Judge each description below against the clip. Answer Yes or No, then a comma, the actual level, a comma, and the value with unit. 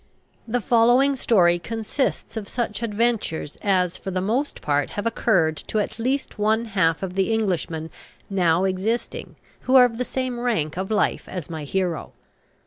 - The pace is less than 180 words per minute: Yes, average, 165 wpm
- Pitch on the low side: No, high, 205 Hz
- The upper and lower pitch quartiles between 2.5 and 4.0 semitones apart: No, average, 4.7 semitones